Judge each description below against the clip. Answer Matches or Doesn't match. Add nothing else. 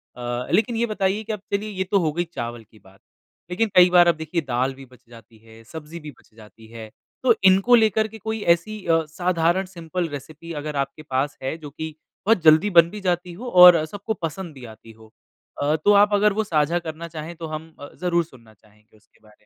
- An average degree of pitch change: Doesn't match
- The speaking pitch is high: Doesn't match